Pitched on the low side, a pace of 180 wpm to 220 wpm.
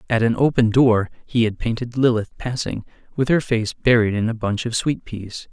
Yes: low, 115 Hz; fast, 205 wpm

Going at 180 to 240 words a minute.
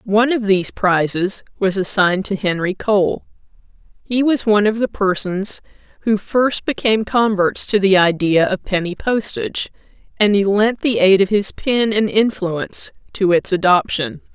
No: average, 160 wpm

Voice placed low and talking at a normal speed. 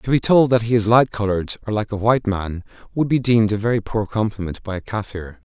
No: low, 110 Hz; fast, 250 wpm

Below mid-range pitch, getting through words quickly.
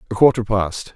No: low, 105 Hz; average, 190 wpm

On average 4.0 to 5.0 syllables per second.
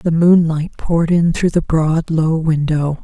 Yes: 4.1 syllables/s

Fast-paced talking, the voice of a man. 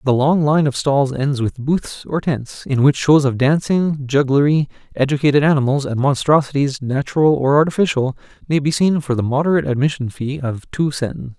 No: average, 180 wpm; male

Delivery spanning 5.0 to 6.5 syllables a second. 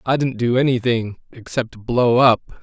No: 4.5 syllables/s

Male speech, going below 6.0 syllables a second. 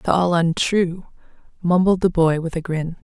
No: female; 4.5 syllables/s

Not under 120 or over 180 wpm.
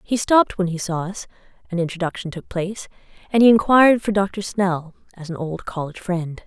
No: average, 195 wpm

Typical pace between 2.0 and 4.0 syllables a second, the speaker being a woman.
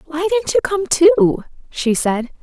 Yes: 3.9 syllables/s; female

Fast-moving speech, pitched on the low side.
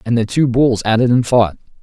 Yes: fast, 265 wpm; low, 115 Hz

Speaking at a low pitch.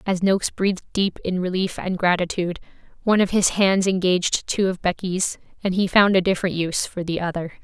No: medium, 185 Hz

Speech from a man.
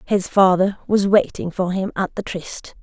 No: female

